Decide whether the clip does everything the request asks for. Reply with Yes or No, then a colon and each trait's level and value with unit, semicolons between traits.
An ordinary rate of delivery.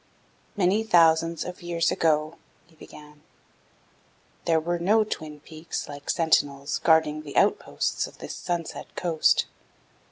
No: slow, 125 wpm